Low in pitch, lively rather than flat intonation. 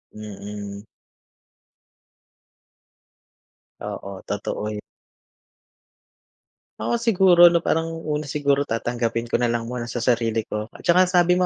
Yes: low, 120 Hz; wide, 7.6 semitones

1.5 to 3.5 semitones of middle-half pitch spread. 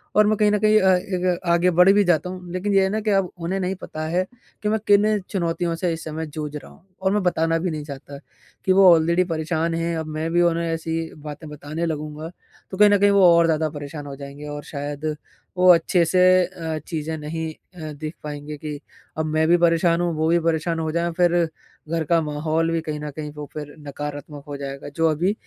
Yes: average, 2.8 semitones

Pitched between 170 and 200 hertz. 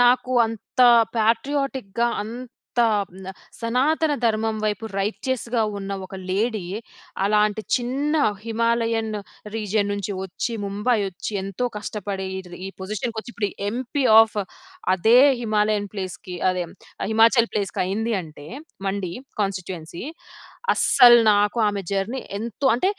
No: high, 215 Hz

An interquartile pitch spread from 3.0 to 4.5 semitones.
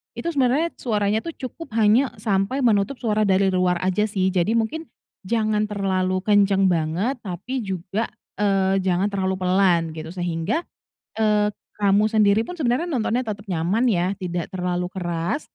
Yes: average, 3.4 semitones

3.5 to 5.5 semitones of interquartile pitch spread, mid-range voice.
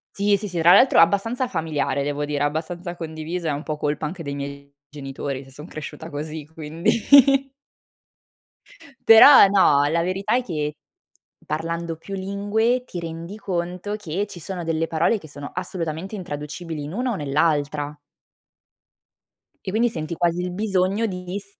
Yes: average, 4.6 semitones; medium, 170 Hz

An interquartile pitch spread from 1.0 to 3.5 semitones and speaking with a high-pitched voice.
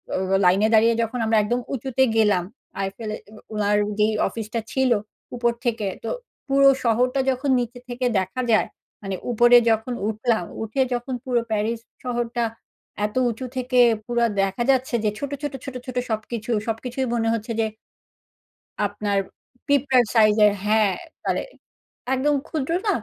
Yes: average, 2.8 semitones; high, 235 Hz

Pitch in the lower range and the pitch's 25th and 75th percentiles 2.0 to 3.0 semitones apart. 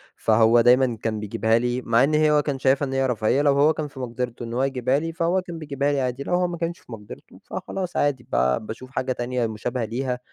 No: low, 130 Hz; average, 3.7 semitones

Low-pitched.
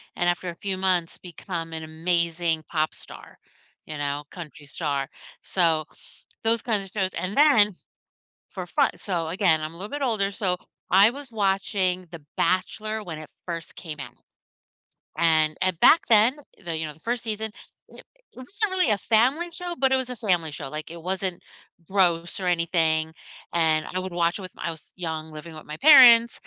No: medium, 180 Hz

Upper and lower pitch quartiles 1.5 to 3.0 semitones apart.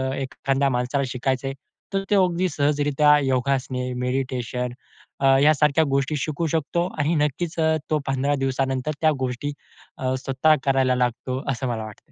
Yes: average, 2.7 semitones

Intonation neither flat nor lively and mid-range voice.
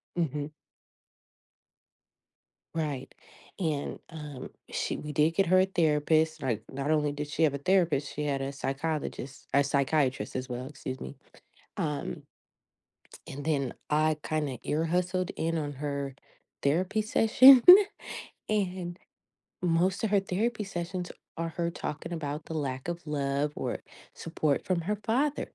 Yes: average, 3.8 semitones; medium, 155 Hz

